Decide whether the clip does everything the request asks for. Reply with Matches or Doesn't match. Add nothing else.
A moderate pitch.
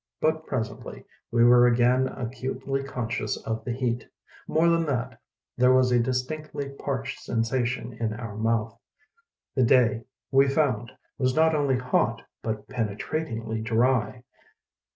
Doesn't match